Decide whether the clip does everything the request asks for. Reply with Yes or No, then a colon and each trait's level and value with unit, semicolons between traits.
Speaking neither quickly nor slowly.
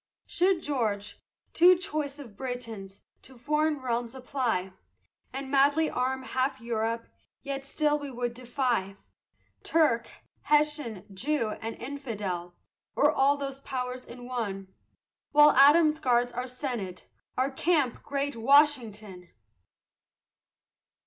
No: slow, 115 wpm